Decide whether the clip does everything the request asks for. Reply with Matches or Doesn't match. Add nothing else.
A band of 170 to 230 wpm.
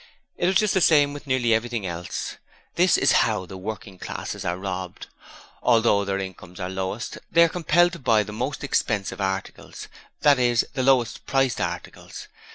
Matches